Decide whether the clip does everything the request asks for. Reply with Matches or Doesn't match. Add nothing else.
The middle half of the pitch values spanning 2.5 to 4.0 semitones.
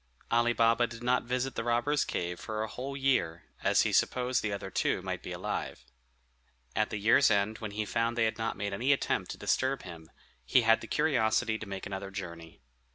Matches